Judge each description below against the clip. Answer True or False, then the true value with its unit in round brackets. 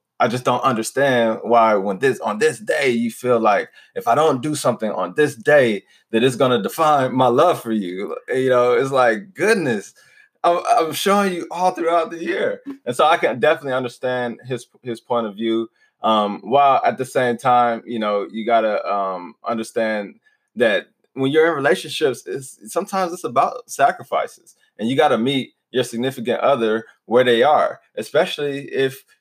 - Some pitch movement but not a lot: False (6.6 semitones)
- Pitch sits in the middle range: False (130 Hz)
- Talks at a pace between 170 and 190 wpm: True (180 wpm)